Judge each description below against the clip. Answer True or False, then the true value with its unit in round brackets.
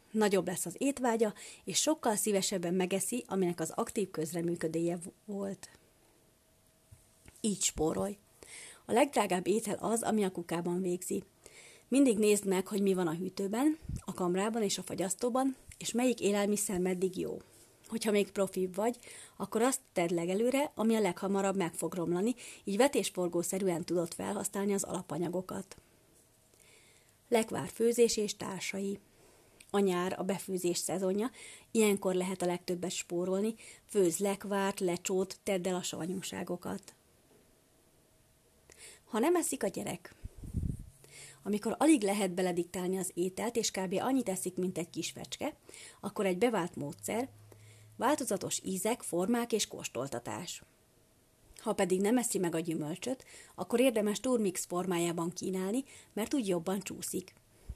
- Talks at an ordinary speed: True (130 wpm)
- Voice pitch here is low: False (195 Hz)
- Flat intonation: False (3.3 semitones)